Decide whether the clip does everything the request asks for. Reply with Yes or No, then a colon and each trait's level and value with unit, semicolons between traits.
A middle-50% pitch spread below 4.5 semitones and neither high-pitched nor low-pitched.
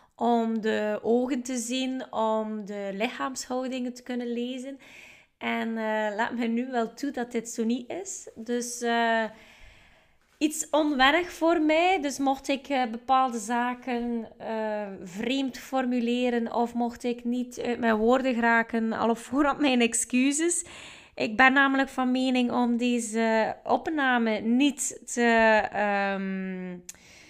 No: narrow, 2.6 semitones; high, 240 Hz